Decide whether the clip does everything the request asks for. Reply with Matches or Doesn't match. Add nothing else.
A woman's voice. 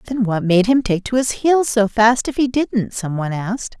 Matches